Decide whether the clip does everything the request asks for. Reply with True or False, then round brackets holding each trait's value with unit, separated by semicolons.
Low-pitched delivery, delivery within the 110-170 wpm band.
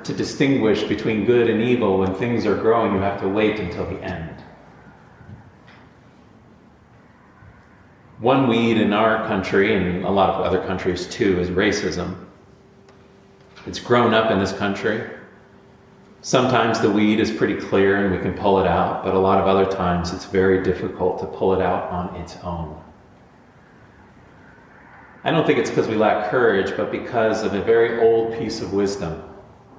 True (95 Hz; 165 wpm)